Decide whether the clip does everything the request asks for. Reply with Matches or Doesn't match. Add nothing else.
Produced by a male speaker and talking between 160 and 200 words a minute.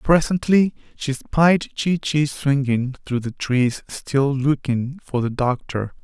Doesn't match